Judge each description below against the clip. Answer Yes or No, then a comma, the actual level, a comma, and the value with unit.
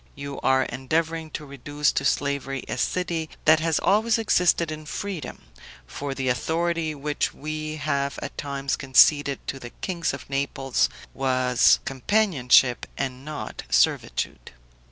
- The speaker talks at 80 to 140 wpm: Yes, slow, 135 wpm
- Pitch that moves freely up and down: No, average, 2.9 semitones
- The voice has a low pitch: No, medium, 145 Hz